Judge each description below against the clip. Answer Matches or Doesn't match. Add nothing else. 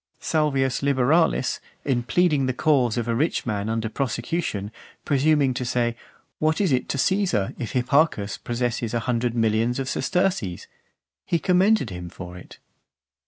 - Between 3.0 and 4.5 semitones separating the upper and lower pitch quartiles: Doesn't match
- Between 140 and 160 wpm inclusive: Matches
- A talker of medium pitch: Doesn't match